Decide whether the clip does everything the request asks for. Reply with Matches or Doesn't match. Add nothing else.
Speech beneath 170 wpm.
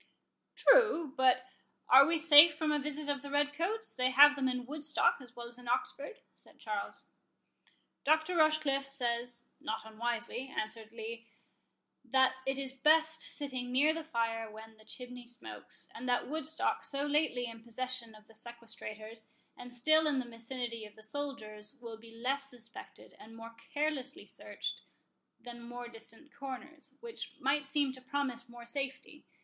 Matches